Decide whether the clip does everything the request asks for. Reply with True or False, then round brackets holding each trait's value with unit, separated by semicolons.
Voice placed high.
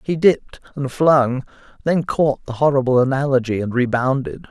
False (135 Hz)